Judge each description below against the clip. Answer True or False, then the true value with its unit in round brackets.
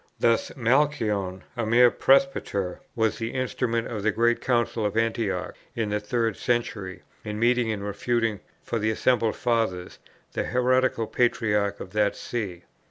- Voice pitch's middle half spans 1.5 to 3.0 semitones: True (2.5 semitones)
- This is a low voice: True (115 Hz)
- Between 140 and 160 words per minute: True (150 wpm)